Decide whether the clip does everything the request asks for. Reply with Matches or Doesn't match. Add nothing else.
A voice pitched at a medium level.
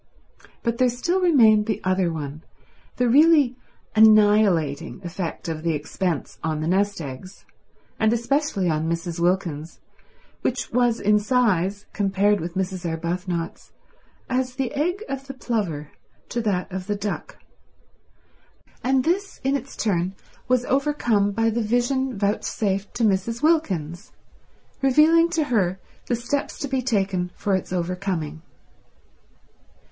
Doesn't match